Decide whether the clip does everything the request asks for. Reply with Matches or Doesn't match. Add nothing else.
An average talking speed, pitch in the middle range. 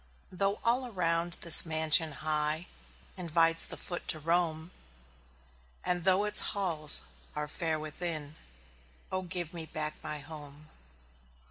Doesn't match